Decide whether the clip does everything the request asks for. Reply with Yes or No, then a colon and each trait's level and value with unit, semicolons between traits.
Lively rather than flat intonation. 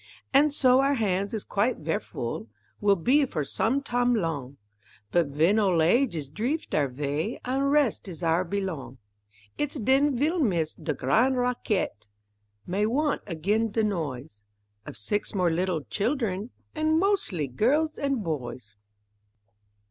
Yes: wide, 8.6 semitones